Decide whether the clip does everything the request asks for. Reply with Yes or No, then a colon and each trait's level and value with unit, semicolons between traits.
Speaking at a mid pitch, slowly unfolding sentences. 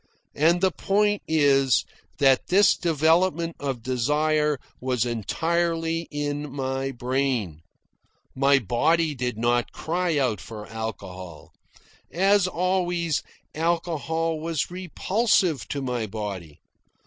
Yes: medium, 145 Hz; slow, 105 wpm